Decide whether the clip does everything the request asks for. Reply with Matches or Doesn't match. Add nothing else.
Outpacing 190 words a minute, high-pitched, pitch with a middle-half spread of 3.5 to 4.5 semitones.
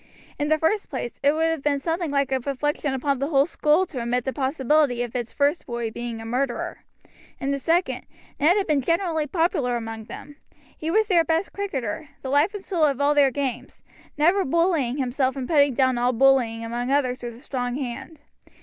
Matches